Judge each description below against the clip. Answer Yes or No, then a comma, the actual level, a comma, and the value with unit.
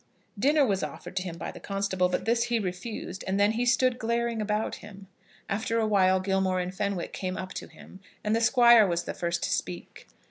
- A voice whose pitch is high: Yes, high, 200 Hz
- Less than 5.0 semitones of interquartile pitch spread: Yes, average, 3.6 semitones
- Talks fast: Yes, fast, 215 wpm